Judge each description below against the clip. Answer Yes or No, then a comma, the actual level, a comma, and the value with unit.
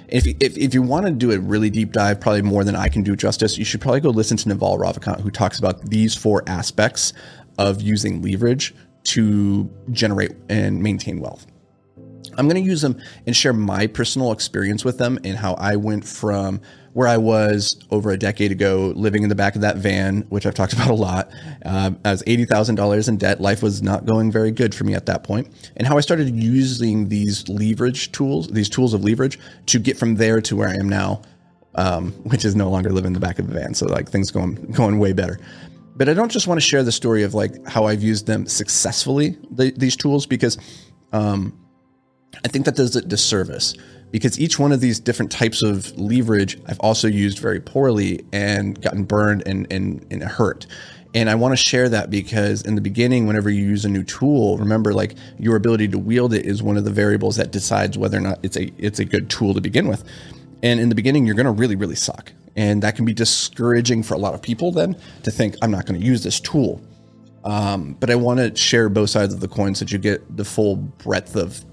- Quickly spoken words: Yes, fast, 230 wpm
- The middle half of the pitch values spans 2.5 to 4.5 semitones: Yes, average, 3.2 semitones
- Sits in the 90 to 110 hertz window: Yes, low, 105 Hz